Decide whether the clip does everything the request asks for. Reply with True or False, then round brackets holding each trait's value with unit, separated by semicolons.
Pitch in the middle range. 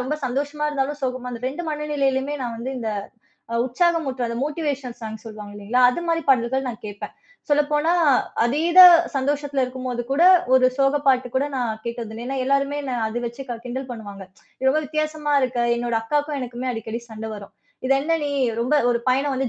False (260 Hz)